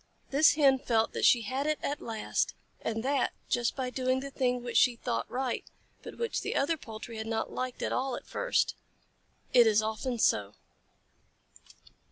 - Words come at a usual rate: Yes, average, 180 wpm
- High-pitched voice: Yes, very high, 250 Hz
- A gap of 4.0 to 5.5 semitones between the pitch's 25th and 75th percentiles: No, average, 3.1 semitones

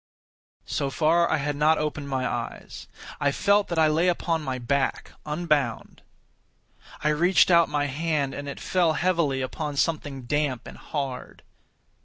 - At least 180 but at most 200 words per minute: No, average, 155 wpm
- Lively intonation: No, average, 3.0 semitones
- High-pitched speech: No, medium, 150 Hz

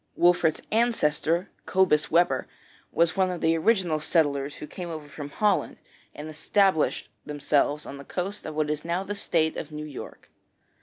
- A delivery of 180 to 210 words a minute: No, average, 165 wpm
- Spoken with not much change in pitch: No, average, 3.3 semitones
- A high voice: No, medium, 160 Hz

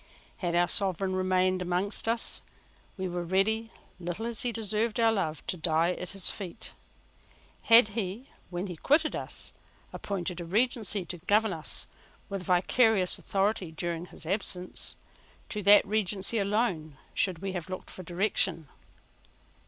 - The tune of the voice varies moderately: Yes, average, 3.3 semitones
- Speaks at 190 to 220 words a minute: No, average, 145 wpm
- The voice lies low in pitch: No, high, 190 Hz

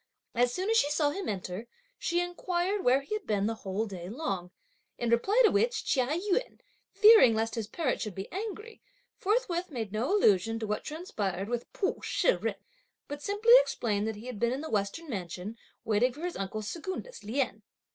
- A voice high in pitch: Yes, very high, 250 Hz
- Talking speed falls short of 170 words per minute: No, average, 195 wpm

